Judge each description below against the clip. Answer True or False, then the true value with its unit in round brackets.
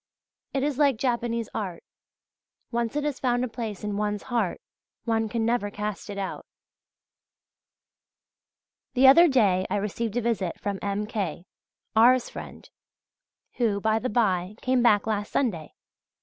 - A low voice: False (225 Hz)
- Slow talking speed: False (150 wpm)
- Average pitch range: True (3.1 semitones)